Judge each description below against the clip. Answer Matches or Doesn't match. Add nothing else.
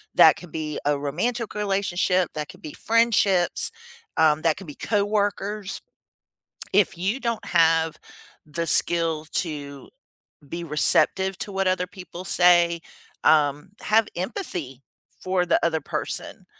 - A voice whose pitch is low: Doesn't match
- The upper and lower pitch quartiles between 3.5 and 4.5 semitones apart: Matches